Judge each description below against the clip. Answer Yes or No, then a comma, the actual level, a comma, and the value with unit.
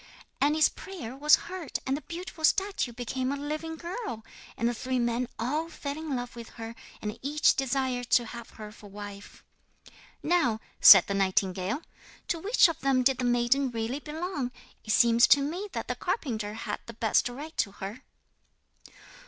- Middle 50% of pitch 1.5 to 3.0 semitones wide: No, average, 4.9 semitones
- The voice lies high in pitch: Yes, very high, 255 Hz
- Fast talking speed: No, average, 175 wpm